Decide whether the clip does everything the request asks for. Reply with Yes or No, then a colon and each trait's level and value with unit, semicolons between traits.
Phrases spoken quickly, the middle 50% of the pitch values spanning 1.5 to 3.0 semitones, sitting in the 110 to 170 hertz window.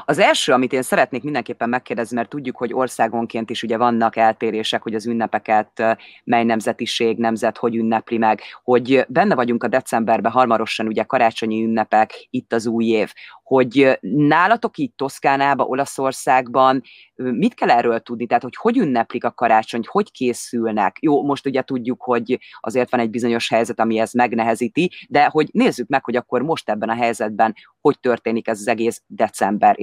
Yes: fast, 170 wpm; narrow, 2.4 semitones; low, 120 Hz